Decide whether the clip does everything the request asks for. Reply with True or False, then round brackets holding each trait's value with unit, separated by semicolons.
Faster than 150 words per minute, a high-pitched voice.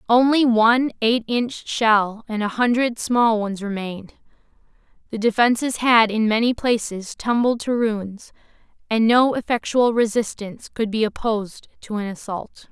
False (140 wpm; 225 Hz)